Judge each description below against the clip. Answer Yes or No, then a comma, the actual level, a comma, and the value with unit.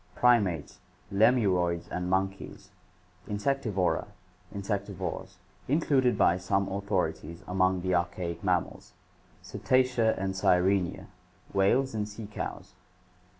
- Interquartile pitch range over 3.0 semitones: Yes, average, 3.4 semitones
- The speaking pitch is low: Yes, very low, 95 Hz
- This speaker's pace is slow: Yes, slow, 95 wpm